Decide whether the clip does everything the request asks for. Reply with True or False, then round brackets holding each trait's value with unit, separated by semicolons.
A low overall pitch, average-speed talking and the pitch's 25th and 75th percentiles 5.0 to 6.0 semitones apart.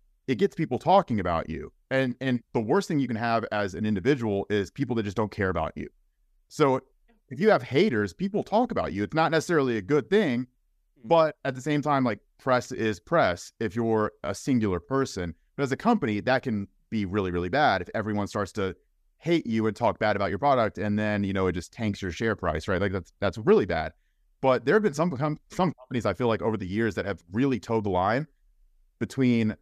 False (115 Hz; 225 wpm; 5.5 semitones)